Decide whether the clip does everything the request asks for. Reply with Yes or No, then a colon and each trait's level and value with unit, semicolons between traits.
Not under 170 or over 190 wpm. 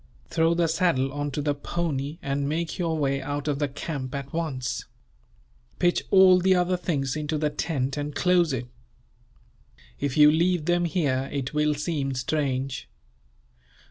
No: average, 160 wpm